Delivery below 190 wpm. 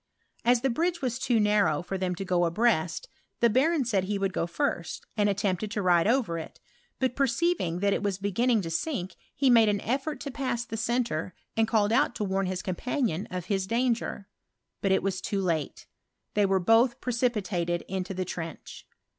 No: average, 195 wpm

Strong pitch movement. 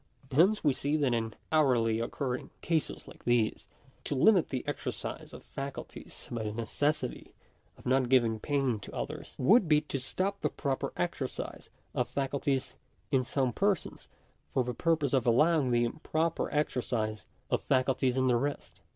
No: average, 3.6 semitones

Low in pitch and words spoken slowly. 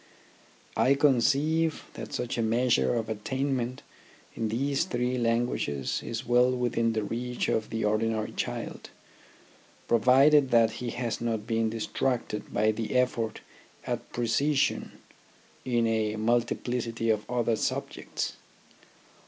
Yes: low, 120 Hz; slow, 125 wpm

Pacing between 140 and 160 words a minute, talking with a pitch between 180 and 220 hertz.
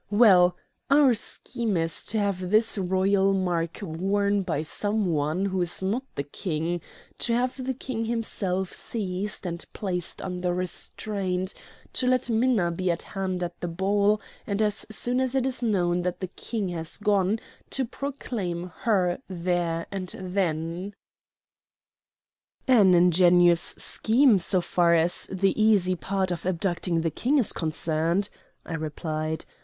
Yes: average, 145 wpm; medium, 185 Hz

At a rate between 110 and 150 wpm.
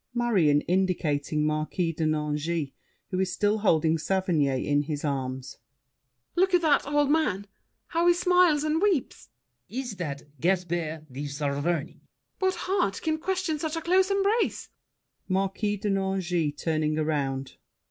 Yes: average, 145 wpm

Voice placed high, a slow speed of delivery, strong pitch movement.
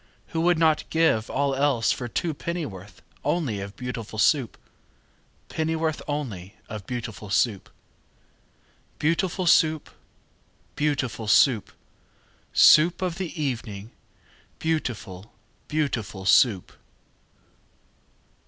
No: low, 135 Hz; slow, 120 wpm; wide, 6.6 semitones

